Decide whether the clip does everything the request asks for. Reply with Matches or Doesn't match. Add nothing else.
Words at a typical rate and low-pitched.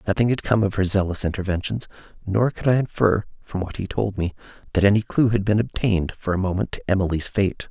Doesn't match